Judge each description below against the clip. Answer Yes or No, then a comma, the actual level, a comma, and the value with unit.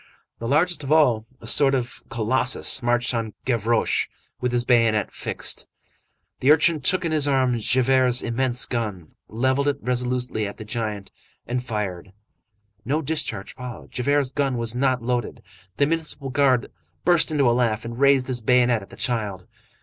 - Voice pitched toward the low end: Yes, low, 125 Hz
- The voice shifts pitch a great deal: No, average, 2.8 semitones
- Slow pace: No, average, 165 wpm